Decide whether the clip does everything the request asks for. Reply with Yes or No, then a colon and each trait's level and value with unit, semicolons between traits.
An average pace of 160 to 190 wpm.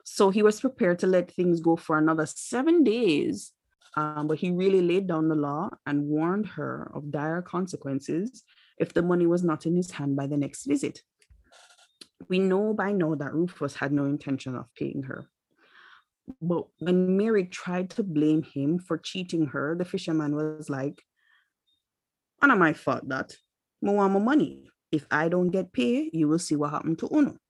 Yes: average, 185 wpm